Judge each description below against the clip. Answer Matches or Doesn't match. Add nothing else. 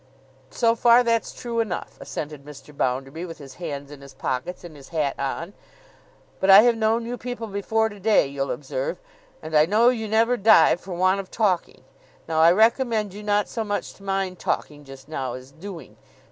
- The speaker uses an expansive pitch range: Matches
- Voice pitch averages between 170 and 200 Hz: Matches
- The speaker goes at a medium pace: Matches